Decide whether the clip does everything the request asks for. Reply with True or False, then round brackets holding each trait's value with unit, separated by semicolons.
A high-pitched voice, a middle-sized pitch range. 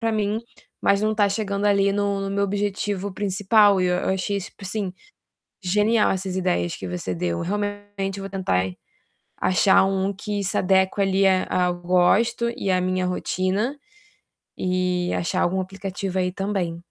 False (195 Hz; 1.9 semitones)